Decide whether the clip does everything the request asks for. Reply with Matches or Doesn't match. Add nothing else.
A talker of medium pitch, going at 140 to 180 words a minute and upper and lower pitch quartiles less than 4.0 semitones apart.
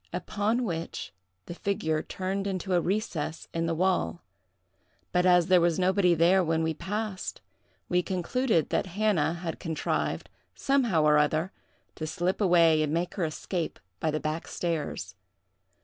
Matches